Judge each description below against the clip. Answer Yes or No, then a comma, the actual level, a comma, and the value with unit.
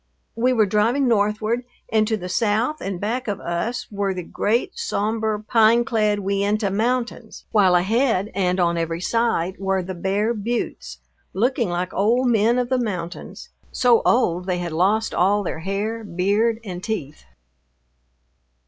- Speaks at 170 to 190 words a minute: No, average, 155 wpm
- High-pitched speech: Yes, high, 210 Hz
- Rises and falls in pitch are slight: No, average, 3.5 semitones